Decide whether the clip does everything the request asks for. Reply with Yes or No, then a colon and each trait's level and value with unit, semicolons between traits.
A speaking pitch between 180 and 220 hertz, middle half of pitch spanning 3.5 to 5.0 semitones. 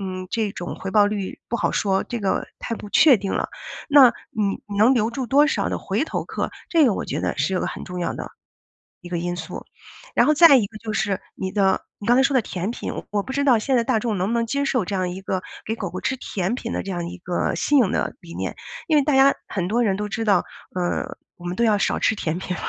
Yes: high, 210 Hz; average, 4.5 semitones